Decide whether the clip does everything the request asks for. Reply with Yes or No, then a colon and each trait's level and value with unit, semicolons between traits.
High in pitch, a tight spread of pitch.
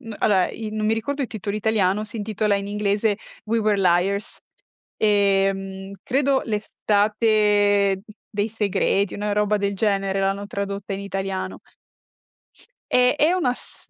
Yes: high, 205 Hz; narrow, 1.6 semitones